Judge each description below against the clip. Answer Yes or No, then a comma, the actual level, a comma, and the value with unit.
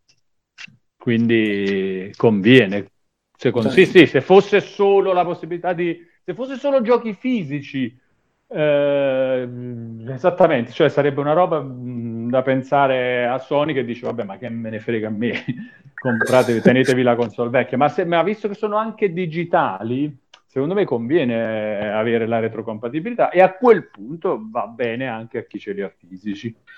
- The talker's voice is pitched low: Yes, low, 130 Hz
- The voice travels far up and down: Yes, wide, 7.5 semitones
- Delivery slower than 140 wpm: No, average, 150 wpm